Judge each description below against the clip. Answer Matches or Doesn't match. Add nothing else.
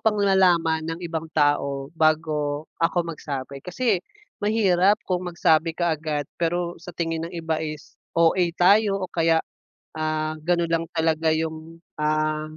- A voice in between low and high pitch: Matches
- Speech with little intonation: Matches